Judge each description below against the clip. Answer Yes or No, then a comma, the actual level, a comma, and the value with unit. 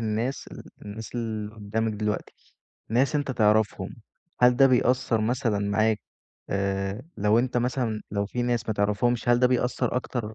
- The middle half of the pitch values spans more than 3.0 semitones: No, average, 2.7 semitones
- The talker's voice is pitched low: Yes, low, 110 Hz